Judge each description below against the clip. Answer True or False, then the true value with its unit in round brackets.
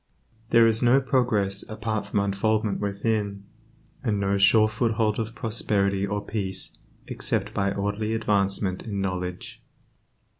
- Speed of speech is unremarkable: False (125 wpm)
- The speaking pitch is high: False (105 Hz)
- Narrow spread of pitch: True (2.1 semitones)